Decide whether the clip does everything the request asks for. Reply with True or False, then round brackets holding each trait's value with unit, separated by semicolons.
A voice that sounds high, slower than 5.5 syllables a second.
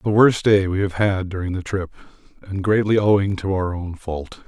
False (95 Hz; 5.0 syllables/s)